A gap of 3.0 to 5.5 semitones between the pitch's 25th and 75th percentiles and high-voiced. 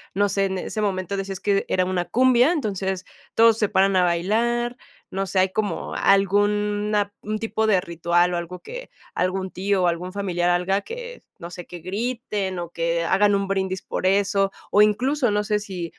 No: narrow, 2.4 semitones; high, 195 Hz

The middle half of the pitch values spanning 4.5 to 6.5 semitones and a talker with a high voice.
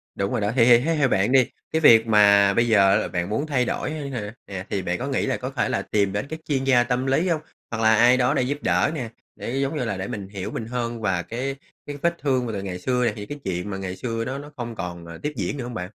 No: average, 4.8 semitones; low, 120 Hz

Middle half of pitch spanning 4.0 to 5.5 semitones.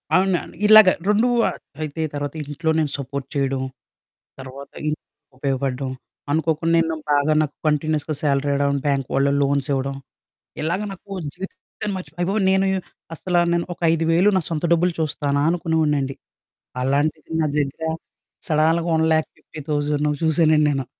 No: average, 2.8 semitones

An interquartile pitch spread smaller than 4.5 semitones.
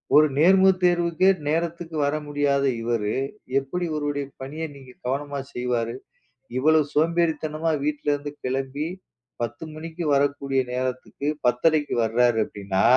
Yes: average, 3.8 semitones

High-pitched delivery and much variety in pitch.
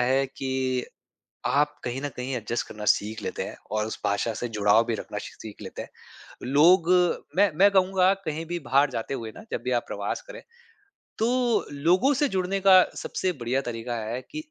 No: low, 135 Hz; wide, 8.0 semitones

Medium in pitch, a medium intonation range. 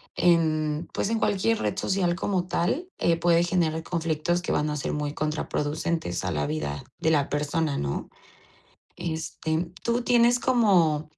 Yes: medium, 165 Hz; average, 3.2 semitones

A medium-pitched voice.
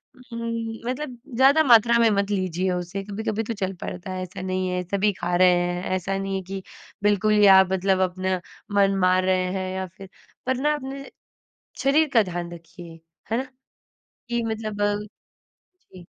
No: high, 195 Hz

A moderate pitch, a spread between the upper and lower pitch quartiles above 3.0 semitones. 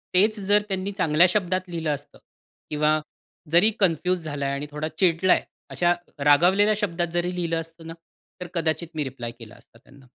Yes: medium, 170 Hz; average, 3.5 semitones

